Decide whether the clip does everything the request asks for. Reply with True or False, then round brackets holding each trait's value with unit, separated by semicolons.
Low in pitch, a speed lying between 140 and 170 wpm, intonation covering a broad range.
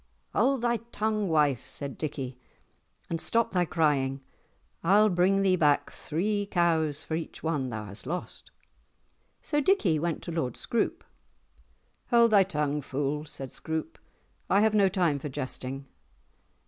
False (165 Hz; 150 wpm; 6.0 semitones)